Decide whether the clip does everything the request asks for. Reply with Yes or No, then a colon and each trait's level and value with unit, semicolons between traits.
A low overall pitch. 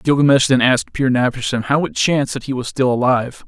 Yes: low, 130 Hz